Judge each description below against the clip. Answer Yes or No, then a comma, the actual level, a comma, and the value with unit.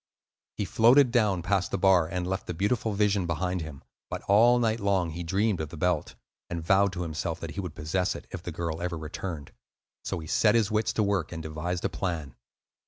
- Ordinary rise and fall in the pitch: Yes, average, 3.5 semitones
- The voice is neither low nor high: No, very low, 90 Hz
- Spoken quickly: Yes, fast, 220 wpm